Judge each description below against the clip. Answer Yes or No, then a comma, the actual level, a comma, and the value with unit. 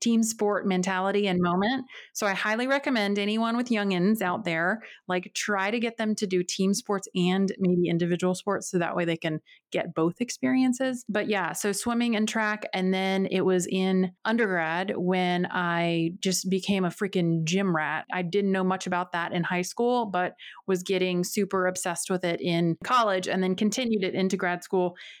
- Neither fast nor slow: Yes, average, 190 wpm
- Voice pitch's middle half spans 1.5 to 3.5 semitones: Yes, average, 2.9 semitones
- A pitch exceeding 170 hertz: Yes, high, 190 Hz